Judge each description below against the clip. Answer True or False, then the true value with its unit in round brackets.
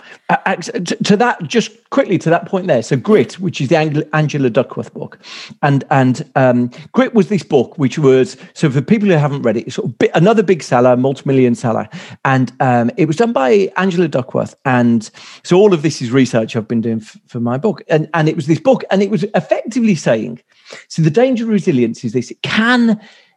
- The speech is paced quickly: True (220 wpm)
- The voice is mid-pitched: True (160 Hz)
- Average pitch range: False (7.8 semitones)